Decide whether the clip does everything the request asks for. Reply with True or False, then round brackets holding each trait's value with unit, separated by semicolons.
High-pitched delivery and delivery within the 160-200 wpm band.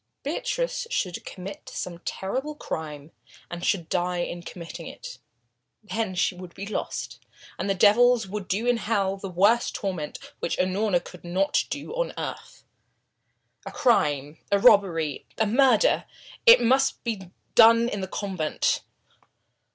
False (195 Hz; 140 wpm)